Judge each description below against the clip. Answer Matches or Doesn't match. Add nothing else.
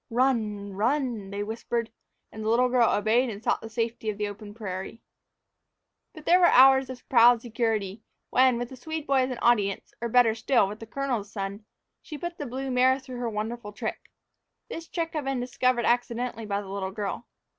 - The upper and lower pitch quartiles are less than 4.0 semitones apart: Matches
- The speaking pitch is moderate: Doesn't match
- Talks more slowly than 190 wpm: Doesn't match